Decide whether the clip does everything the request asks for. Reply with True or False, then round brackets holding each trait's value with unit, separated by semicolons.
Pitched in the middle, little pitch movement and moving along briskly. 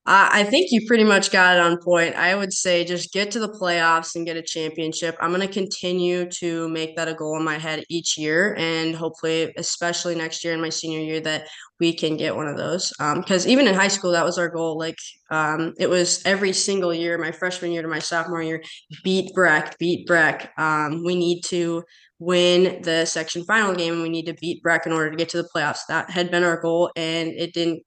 True (170 Hz; 1.6 semitones; 235 wpm)